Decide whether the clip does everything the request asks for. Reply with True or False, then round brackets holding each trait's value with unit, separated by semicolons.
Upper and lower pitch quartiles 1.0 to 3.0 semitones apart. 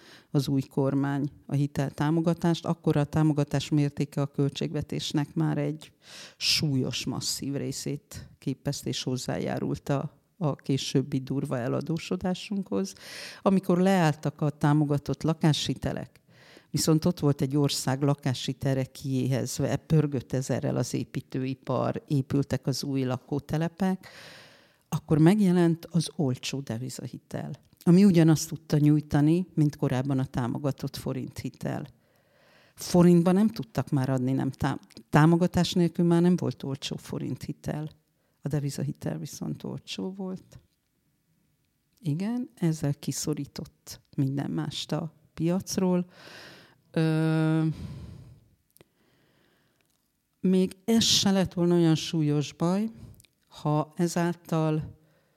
False (3.4 semitones)